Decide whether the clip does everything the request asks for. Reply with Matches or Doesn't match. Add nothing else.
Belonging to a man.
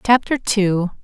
Doesn't match